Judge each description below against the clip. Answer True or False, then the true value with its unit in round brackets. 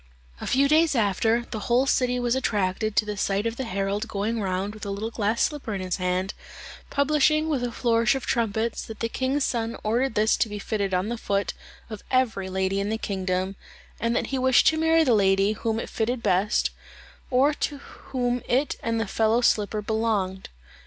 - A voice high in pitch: True (225 Hz)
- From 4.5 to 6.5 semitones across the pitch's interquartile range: False (3.8 semitones)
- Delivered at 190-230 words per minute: True (200 wpm)